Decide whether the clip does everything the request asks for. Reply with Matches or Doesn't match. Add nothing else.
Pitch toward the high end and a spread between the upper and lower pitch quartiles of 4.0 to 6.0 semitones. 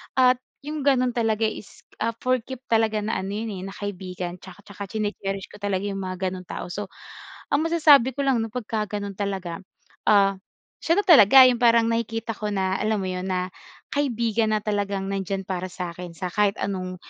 Doesn't match